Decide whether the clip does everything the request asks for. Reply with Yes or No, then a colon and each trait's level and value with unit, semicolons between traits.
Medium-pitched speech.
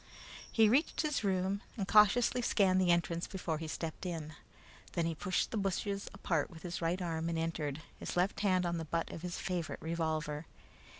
Yes: medium, 175 Hz